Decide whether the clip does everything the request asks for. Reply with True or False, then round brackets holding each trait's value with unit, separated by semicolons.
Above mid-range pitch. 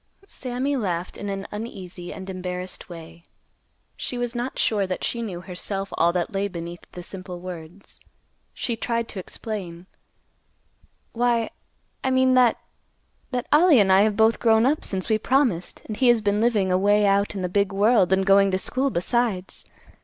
True (200 Hz)